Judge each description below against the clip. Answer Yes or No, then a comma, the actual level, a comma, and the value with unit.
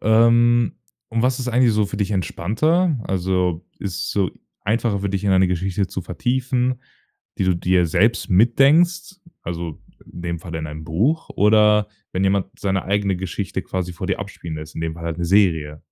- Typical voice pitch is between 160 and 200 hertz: No, very low, 95 Hz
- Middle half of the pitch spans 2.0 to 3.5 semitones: No, average, 4.9 semitones